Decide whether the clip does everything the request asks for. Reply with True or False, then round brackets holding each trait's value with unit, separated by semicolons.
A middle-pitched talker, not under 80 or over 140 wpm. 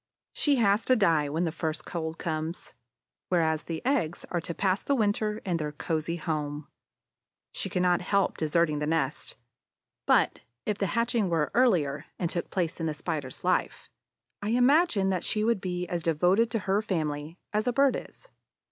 False (175 Hz; 175 wpm)